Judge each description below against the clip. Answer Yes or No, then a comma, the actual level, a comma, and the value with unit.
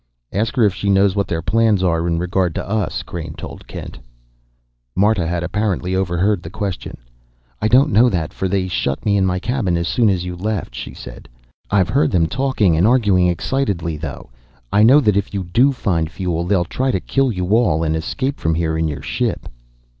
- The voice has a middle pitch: No, very low, 95 Hz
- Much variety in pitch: No, average, 4.1 semitones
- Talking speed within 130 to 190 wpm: No, fast, 205 wpm